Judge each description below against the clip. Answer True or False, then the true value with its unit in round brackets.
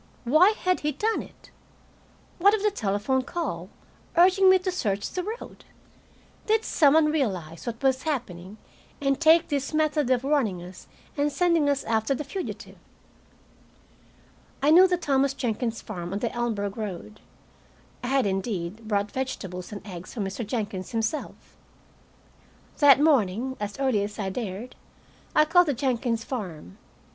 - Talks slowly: False (155 wpm)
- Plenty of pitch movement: True (6.9 semitones)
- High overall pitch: True (255 Hz)